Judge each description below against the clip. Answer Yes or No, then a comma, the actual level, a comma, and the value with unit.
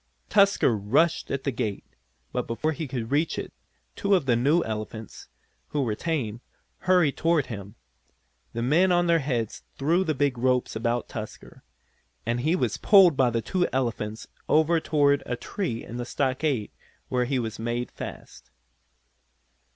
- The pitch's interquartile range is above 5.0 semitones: Yes, wide, 5.4 semitones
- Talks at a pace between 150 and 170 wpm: Yes, average, 160 wpm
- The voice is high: No, low, 130 Hz